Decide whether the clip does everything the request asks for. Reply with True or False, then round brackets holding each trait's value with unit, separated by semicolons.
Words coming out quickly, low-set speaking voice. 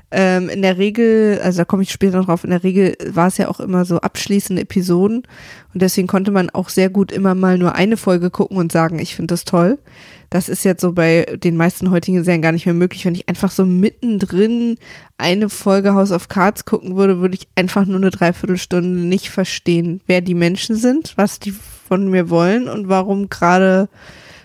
False (210 wpm; 185 Hz)